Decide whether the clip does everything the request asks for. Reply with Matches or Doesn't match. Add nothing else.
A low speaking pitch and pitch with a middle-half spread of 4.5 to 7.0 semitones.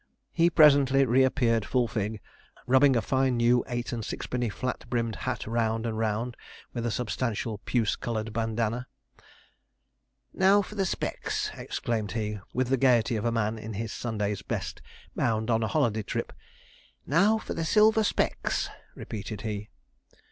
Doesn't match